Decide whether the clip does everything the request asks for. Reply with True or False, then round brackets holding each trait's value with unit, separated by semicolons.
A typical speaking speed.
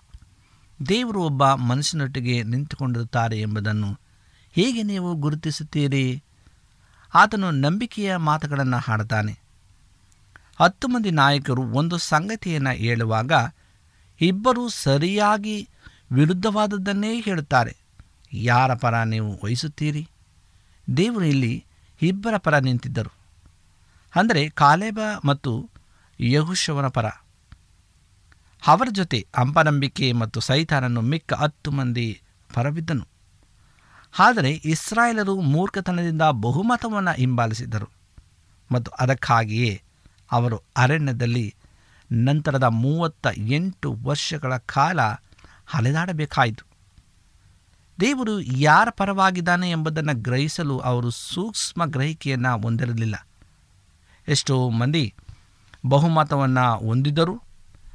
True (75 wpm)